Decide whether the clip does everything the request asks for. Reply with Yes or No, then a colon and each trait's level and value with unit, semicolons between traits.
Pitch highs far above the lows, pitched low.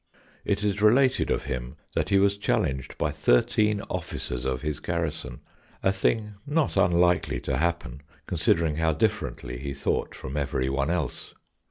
Yes: wide, 6.7 semitones; very low, 85 Hz